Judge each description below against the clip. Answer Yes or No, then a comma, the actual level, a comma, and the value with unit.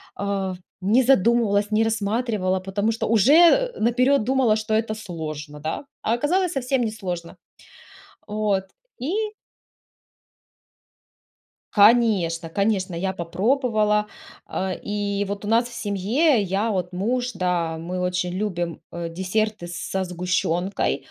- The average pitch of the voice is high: Yes, high, 205 Hz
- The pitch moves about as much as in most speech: Yes, average, 4.0 semitones